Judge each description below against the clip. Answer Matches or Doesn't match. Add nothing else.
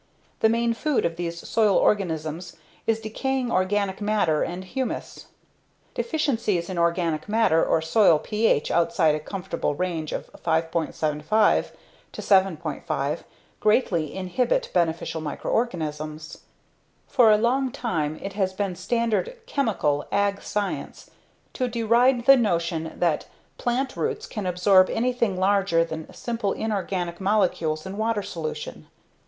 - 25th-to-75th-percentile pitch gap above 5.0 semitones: Matches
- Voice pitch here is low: Doesn't match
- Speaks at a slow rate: Matches